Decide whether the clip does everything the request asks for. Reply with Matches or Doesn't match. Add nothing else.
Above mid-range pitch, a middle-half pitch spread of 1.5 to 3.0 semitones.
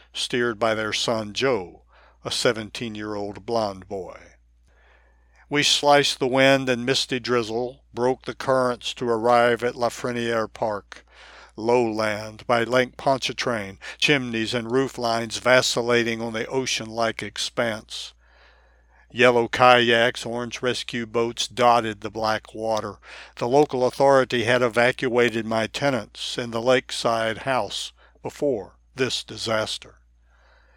Doesn't match